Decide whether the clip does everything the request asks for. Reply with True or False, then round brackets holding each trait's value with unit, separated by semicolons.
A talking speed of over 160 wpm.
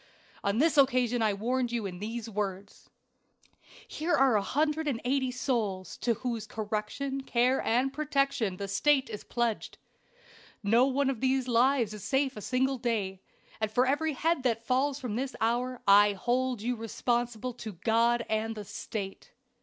False (155 wpm)